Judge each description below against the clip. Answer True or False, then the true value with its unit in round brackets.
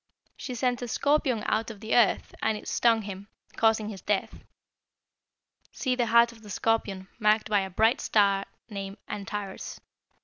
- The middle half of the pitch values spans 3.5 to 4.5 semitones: False (2.6 semitones)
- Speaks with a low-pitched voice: False (220 Hz)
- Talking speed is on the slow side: False (170 wpm)